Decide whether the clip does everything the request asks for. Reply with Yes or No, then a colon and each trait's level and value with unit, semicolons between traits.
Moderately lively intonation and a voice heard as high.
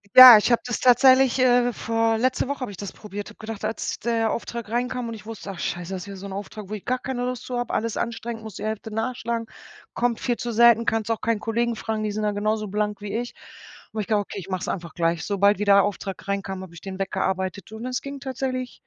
Yes: average, 3.1 semitones; high, 220 Hz